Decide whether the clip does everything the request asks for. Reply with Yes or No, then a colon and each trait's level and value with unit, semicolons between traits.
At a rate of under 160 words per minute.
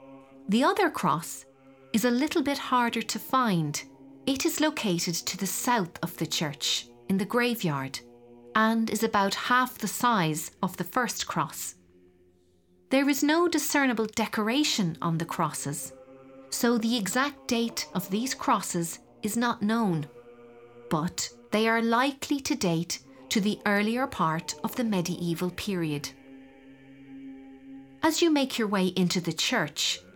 Yes: average, 145 wpm